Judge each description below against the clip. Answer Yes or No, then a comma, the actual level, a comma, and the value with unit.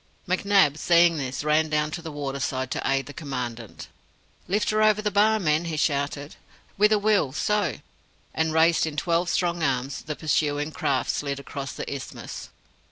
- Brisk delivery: No, average, 175 wpm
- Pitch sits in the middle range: Yes, medium, 155 Hz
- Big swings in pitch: No, average, 4.0 semitones